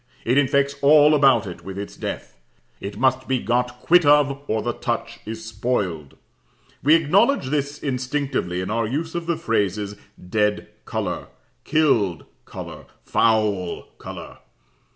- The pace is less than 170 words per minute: Yes, average, 140 wpm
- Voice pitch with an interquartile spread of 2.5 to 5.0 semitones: No, wide, 5.6 semitones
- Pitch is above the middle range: No, low, 125 Hz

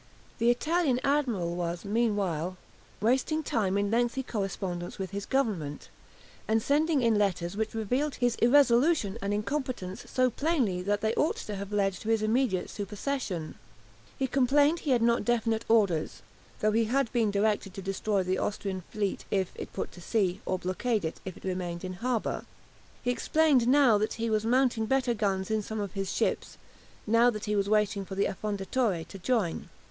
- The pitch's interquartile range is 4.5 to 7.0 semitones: No, average, 4.1 semitones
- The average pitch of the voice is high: Yes, high, 215 Hz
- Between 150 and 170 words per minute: No, average, 180 wpm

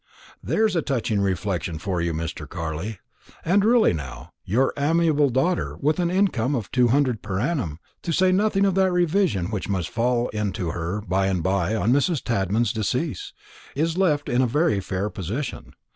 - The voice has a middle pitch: No, low, 120 Hz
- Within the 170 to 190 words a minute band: Yes, average, 185 wpm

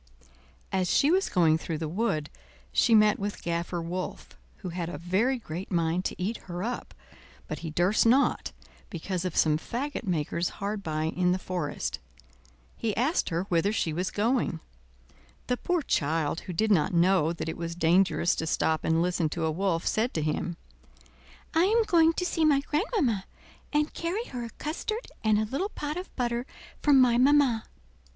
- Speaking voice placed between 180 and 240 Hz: Yes, high, 190 Hz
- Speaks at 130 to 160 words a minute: No, average, 180 wpm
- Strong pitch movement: Yes, wide, 7.1 semitones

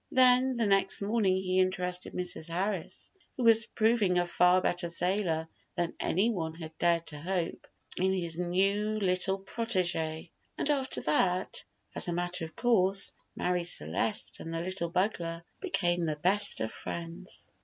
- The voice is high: No, medium, 180 Hz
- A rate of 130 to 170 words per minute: Yes, average, 155 wpm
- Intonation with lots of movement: No, average, 2.8 semitones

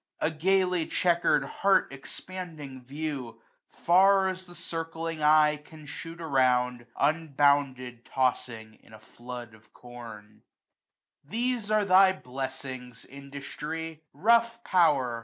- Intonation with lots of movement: Yes, wide, 5.8 semitones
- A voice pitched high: No, medium, 150 Hz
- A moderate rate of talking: No, slow, 115 wpm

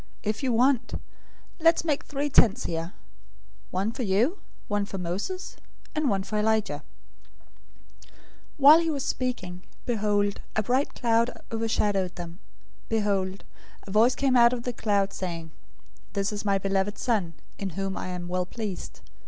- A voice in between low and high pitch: No, high, 210 Hz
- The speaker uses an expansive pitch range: No, average, 4.3 semitones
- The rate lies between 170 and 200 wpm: No, average, 155 wpm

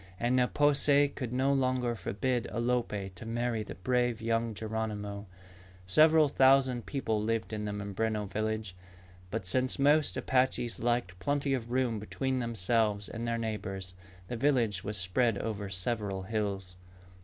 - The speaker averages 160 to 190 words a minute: No, average, 150 wpm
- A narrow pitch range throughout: No, average, 3.6 semitones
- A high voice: No, low, 115 Hz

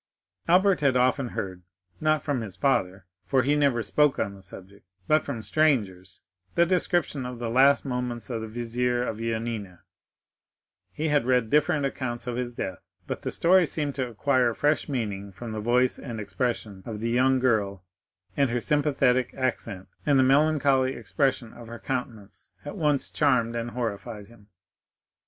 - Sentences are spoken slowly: No, average, 165 wpm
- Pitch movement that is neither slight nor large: Yes, average, 4.2 semitones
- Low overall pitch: Yes, low, 125 Hz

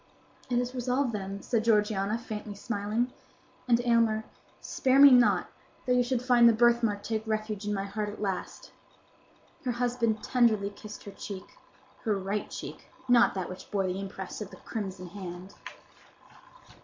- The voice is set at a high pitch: Yes, high, 215 Hz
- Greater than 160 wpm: No, average, 155 wpm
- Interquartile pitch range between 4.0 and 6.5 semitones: No, average, 3.1 semitones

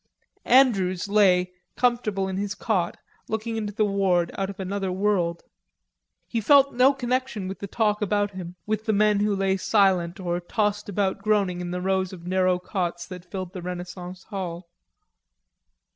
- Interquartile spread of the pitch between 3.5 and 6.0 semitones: No, narrow, 2.6 semitones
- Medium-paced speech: Yes, average, 165 wpm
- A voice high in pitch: Yes, high, 195 Hz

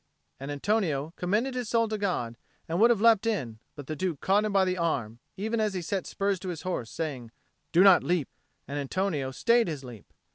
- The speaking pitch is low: No, medium, 180 Hz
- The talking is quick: Yes, fast, 215 wpm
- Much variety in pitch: Yes, wide, 6.5 semitones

